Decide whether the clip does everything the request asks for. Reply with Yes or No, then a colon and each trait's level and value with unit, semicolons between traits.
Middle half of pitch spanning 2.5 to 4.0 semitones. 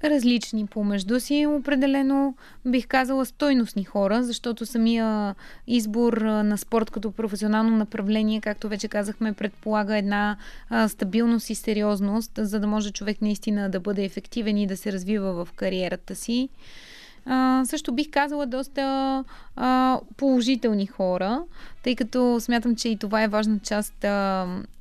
Yes: average, 3.4 semitones